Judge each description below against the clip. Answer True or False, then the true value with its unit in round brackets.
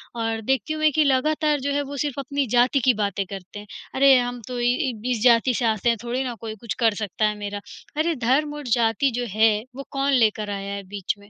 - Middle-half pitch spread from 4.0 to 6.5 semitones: True (4.3 semitones)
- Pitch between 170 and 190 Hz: False (240 Hz)